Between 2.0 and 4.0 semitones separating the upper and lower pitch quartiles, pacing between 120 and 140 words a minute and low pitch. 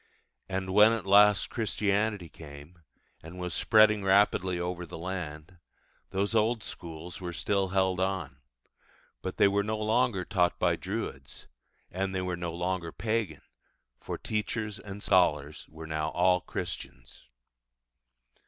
Yes: average, 3.3 semitones; slow, 135 wpm; very low, 95 Hz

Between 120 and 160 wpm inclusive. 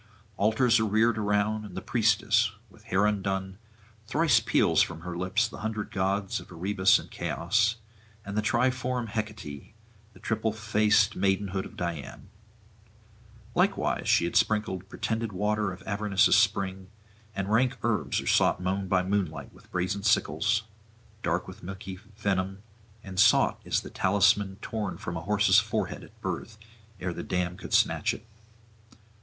Yes: average, 150 wpm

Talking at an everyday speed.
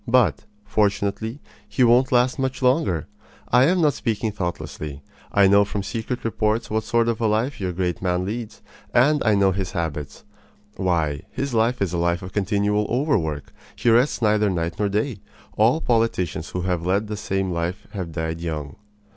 Yes: average, 180 wpm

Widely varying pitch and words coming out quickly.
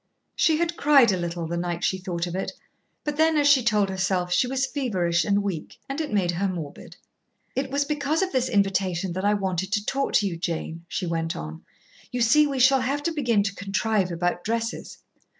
Yes: wide, 7.3 semitones; fast, 215 wpm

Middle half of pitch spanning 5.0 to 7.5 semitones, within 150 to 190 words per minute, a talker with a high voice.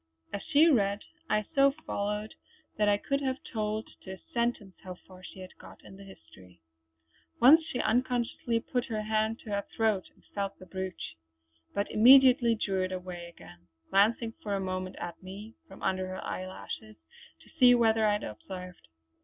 No: average, 3.7 semitones; average, 180 wpm; high, 205 Hz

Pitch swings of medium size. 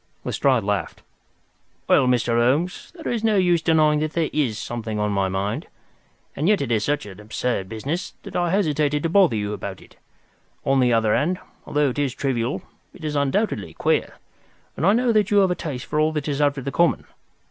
No: wide, 6.4 semitones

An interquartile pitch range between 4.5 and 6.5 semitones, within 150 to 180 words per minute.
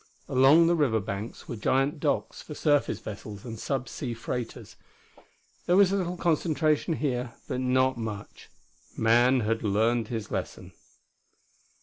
No: average, 5.0 semitones; average, 140 wpm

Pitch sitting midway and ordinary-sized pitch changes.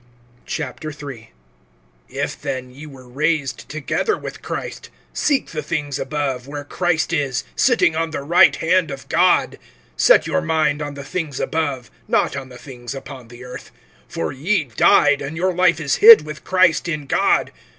Yes: medium, 145 Hz; average, 3.3 semitones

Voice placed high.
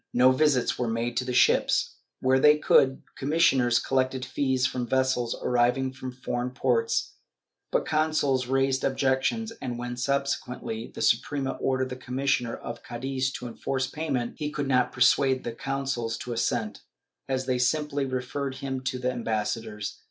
No: low, 130 Hz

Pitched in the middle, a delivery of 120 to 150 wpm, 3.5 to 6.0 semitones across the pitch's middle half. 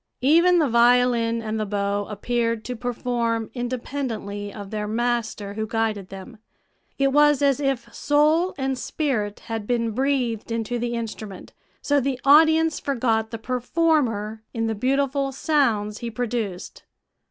No: high, 235 Hz; average, 140 wpm; average, 3.8 semitones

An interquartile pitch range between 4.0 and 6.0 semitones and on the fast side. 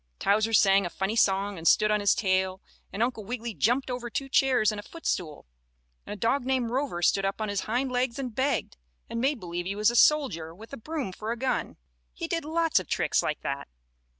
Yes: average, 4.9 semitones; fast, 225 wpm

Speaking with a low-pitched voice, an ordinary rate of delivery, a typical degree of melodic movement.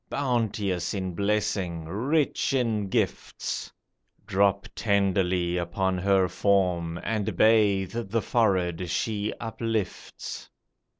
No: low, 100 Hz; slow, 95 wpm; average, 3.2 semitones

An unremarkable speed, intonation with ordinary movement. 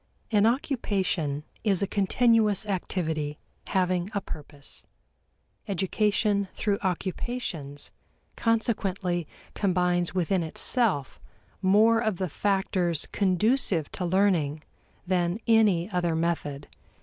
No: slow, 95 wpm; average, 3.4 semitones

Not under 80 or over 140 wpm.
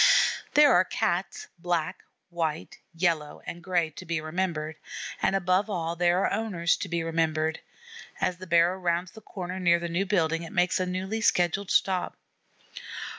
No: average, 165 wpm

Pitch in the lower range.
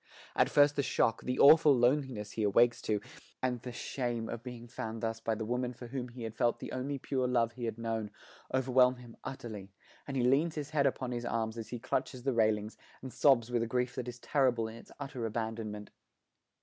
Yes: low, 120 Hz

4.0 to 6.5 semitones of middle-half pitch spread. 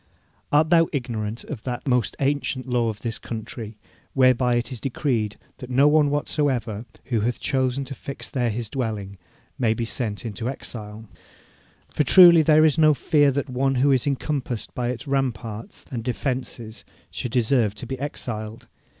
No: average, 3.5 semitones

